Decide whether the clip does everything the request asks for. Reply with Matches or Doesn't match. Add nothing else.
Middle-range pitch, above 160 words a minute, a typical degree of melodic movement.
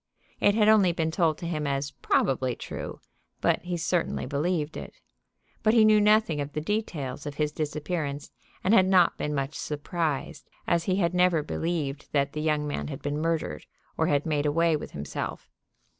Matches